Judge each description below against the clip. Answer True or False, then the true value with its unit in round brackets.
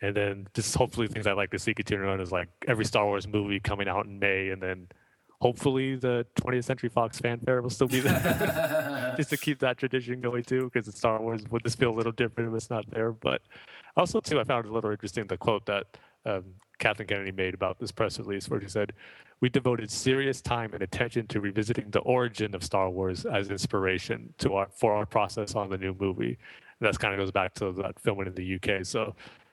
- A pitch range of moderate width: True (3.8 semitones)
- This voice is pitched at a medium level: False (110 Hz)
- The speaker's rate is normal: False (230 wpm)